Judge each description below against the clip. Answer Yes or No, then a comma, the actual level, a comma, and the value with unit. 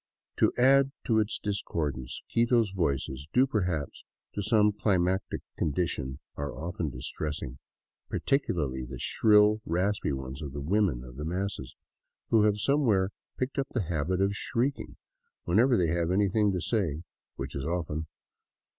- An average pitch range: No, wide, 6.2 semitones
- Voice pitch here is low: Yes, very low, 90 Hz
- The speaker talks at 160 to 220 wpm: No, average, 150 wpm